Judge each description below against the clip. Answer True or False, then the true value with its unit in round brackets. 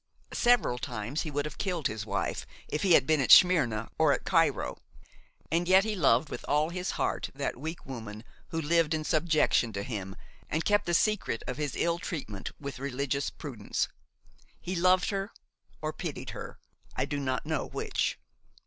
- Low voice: False (150 Hz)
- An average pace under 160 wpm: False (175 wpm)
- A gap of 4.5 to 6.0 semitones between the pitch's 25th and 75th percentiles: True (5.4 semitones)